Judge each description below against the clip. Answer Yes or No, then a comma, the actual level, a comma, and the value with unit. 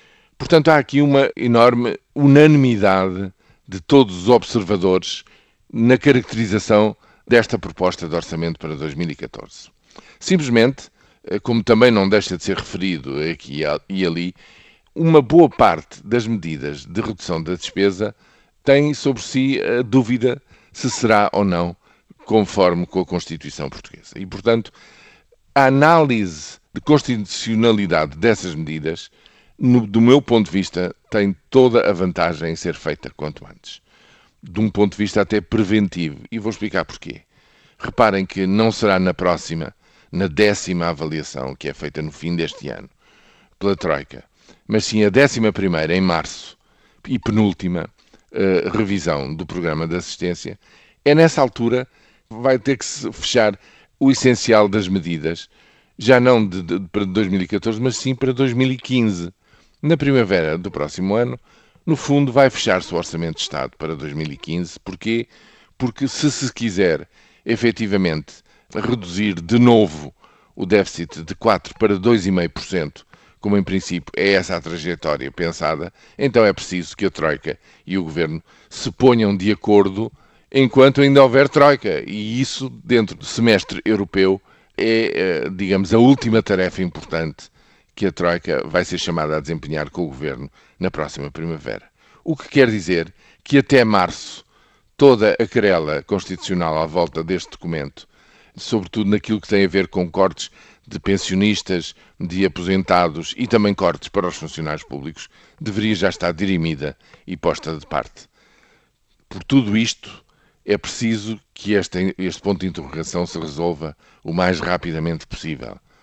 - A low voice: Yes, low, 100 Hz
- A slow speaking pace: No, average, 145 wpm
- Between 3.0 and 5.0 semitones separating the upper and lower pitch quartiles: No, wide, 5.4 semitones